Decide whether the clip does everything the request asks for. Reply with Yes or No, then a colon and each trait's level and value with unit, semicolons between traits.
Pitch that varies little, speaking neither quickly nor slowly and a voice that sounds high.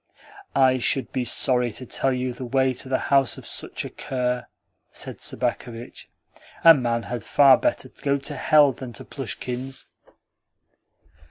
No: narrow, 1.6 semitones; average, 155 wpm; low, 130 Hz